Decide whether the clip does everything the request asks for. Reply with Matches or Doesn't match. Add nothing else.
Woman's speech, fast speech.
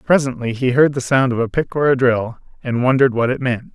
Doesn't match